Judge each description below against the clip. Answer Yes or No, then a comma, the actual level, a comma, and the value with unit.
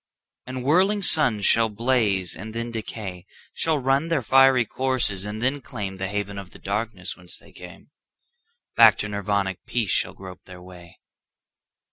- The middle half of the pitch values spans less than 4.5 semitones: No, average, 5.3 semitones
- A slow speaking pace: No, average, 145 wpm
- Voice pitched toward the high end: No, low, 110 Hz